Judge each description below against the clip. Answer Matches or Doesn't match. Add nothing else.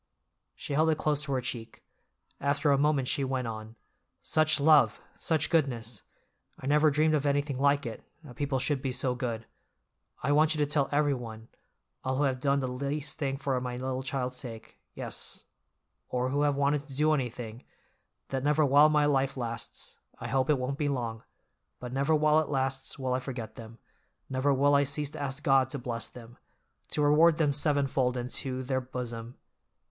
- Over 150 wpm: Matches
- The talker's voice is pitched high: Doesn't match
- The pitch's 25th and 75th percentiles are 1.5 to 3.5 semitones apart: Matches